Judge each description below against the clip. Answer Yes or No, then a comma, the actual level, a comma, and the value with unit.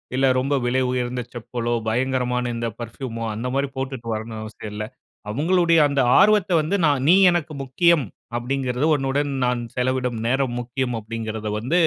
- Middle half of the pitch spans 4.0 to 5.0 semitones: No, average, 2.8 semitones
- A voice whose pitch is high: No, low, 130 Hz